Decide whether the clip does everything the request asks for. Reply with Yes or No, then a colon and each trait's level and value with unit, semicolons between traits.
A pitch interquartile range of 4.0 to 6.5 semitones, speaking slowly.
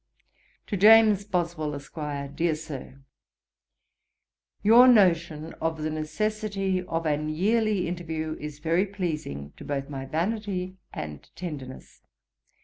Yes: average, 4.7 semitones; slow, 115 wpm